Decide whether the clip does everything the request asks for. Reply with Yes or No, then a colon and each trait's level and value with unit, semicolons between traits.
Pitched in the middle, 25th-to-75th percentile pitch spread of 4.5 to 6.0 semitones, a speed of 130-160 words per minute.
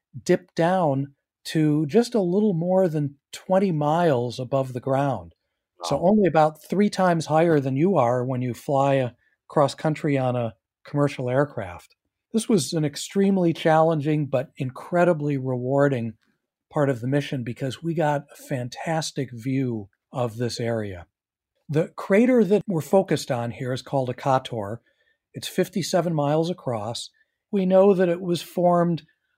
Yes: medium, 145 Hz; average, 5.2 semitones; average, 150 wpm